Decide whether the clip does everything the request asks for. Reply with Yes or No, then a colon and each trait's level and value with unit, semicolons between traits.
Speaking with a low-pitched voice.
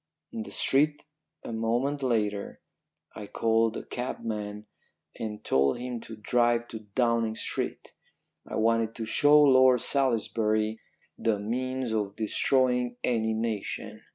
Yes: low, 115 Hz